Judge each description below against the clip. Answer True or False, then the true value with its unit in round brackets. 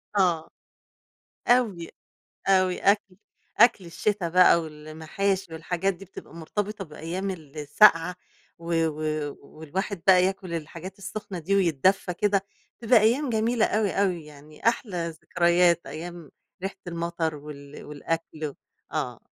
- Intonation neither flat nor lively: True (3.7 semitones)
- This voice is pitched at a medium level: True (175 Hz)